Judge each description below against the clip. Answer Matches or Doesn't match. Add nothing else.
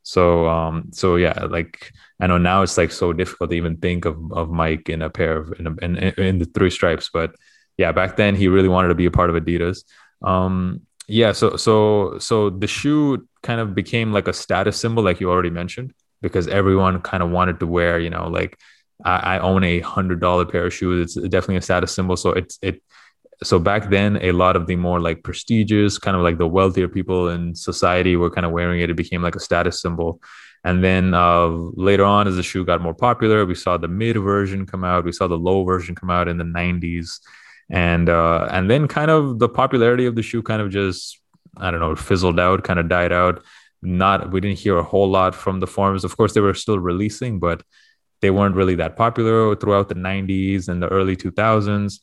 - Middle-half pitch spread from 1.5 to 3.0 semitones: Matches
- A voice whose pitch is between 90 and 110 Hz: Matches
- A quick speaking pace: Matches